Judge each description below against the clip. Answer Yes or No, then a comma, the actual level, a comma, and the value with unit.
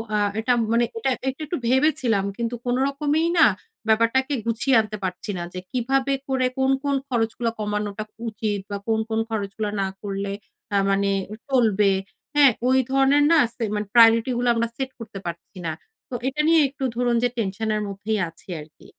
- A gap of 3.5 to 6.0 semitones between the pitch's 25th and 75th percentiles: Yes, average, 4.2 semitones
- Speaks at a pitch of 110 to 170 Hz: No, high, 230 Hz